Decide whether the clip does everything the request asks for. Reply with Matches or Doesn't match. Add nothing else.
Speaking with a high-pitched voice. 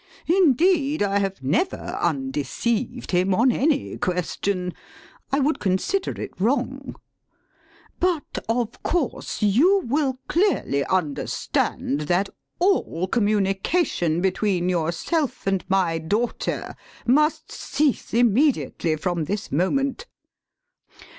Matches